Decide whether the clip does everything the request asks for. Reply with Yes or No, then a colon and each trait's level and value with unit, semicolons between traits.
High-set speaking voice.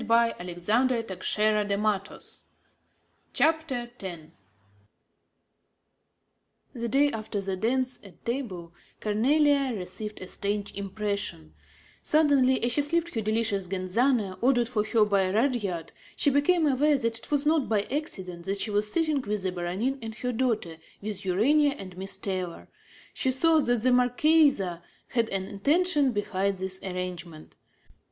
Yes: high, 220 Hz